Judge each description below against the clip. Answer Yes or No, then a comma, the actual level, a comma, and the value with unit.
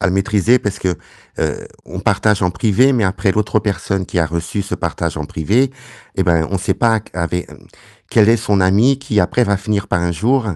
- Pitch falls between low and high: No, low, 100 Hz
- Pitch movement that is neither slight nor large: Yes, average, 3.6 semitones